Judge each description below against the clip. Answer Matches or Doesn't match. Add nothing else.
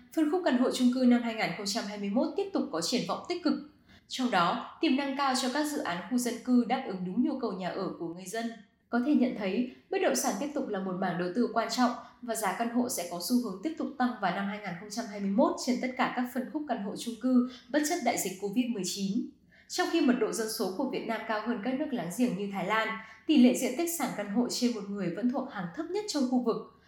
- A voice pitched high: Matches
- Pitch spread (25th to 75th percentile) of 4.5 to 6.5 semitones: Doesn't match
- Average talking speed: Doesn't match